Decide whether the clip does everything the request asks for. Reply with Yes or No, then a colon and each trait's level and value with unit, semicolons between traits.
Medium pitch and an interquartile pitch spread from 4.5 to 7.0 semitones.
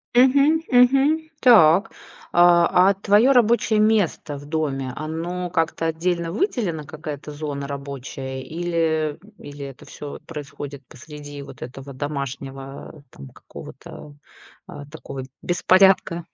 Yes: medium, 160 Hz; average, 5.2 semitones